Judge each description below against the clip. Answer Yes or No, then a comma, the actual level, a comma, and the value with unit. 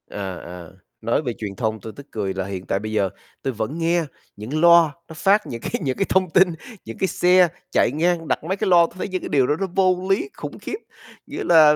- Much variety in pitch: Yes, wide, 8.6 semitones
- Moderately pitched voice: Yes, medium, 155 Hz